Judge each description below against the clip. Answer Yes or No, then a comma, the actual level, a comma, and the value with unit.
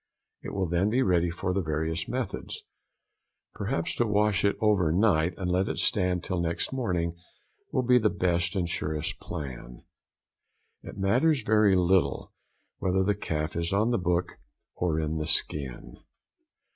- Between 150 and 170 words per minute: Yes, average, 160 wpm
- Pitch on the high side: No, very low, 90 Hz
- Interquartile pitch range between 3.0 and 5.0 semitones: Yes, average, 3.9 semitones